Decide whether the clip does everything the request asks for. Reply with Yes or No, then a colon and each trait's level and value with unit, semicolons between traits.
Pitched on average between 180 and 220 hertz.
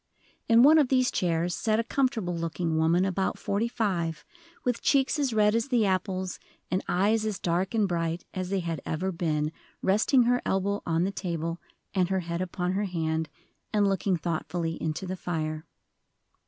Yes: medium, 185 Hz